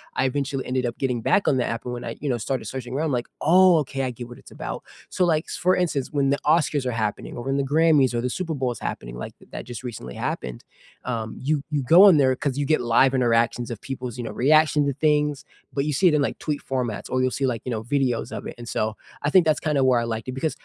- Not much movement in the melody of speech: No, average, 3.6 semitones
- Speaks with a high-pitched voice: No, low, 135 Hz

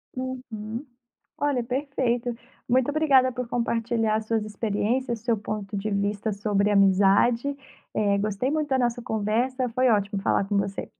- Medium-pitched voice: No, high, 230 Hz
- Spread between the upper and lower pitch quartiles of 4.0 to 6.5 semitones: No, average, 3.6 semitones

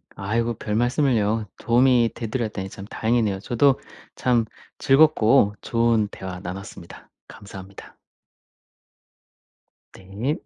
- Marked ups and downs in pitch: No, average, 3.5 semitones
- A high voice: No, low, 115 Hz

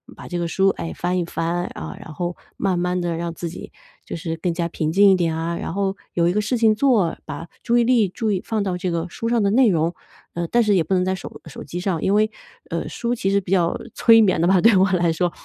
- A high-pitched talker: No, medium, 180 Hz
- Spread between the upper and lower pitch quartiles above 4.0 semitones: No, average, 3.3 semitones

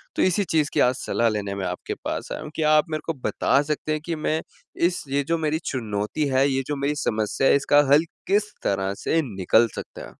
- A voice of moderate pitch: Yes, medium, 145 Hz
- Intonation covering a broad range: Yes, wide, 5.8 semitones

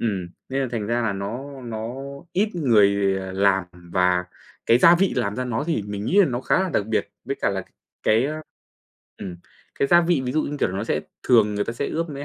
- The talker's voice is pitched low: Yes, low, 115 Hz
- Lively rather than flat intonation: Yes, wide, 5.9 semitones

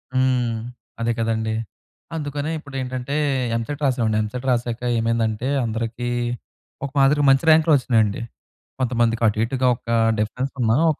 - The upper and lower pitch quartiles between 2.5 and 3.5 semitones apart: Yes, average, 2.9 semitones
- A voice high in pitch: No, low, 120 Hz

